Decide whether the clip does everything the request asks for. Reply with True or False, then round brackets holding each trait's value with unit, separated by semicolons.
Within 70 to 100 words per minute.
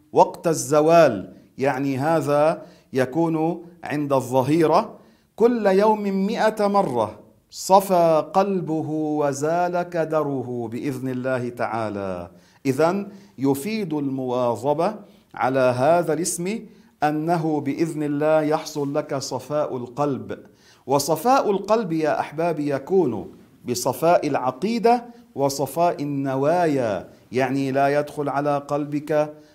True (90 wpm)